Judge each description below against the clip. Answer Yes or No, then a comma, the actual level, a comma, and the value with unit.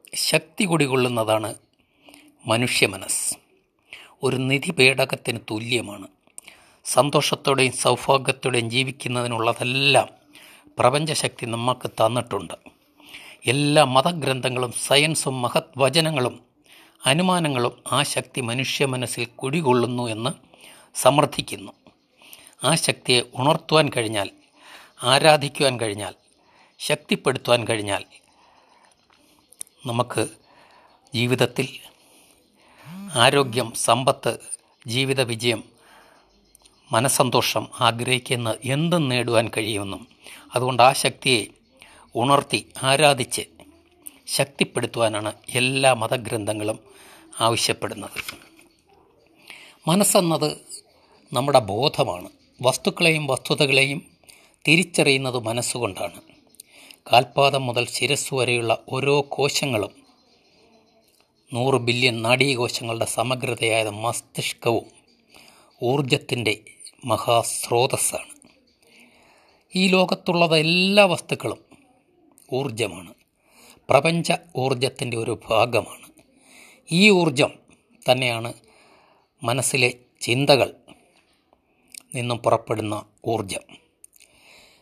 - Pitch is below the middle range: Yes, low, 130 Hz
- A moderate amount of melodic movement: Yes, average, 3.6 semitones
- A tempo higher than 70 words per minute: No, average, 65 wpm